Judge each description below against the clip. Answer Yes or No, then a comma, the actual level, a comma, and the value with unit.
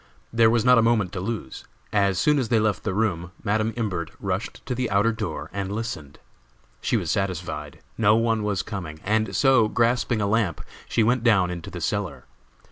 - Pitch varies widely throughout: No, average, 3.7 semitones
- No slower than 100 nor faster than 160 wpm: No, average, 195 wpm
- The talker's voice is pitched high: No, low, 105 Hz